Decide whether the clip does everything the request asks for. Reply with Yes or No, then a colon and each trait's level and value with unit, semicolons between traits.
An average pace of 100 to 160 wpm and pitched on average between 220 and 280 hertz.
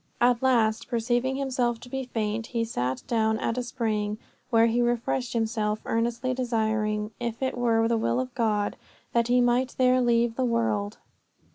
No: average, 170 wpm; high, 230 Hz